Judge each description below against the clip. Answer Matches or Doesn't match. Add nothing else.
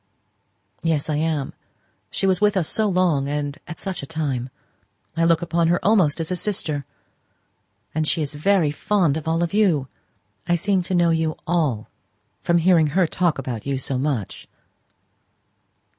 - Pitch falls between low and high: Matches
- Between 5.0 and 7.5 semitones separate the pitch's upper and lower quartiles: Doesn't match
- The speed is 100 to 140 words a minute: Doesn't match